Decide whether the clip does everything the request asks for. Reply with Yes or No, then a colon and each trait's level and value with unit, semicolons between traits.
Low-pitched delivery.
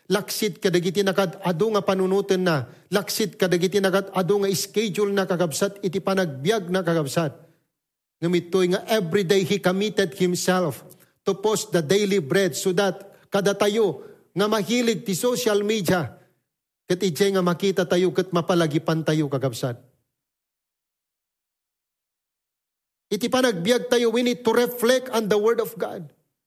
No: high, 195 Hz